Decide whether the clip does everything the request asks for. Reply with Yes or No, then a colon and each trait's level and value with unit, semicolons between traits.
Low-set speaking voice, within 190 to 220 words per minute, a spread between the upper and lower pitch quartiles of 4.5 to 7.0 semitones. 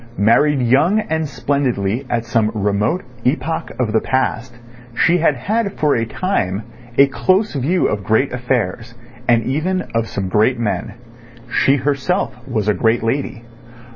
No: low, 125 Hz; average, 150 wpm; average, 4.9 semitones